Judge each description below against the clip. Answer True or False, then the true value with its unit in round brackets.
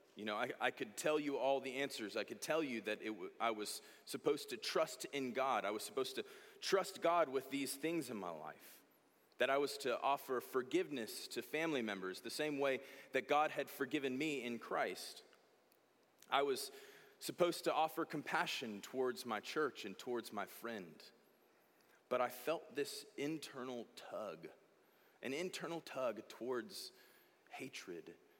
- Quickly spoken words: False (165 wpm)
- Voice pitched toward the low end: False (150 Hz)